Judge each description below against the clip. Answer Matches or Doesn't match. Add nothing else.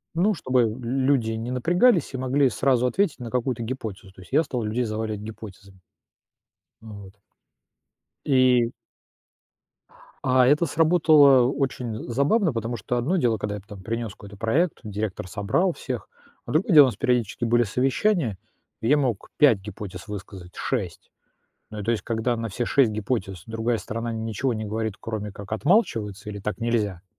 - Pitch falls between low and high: Doesn't match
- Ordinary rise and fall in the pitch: Matches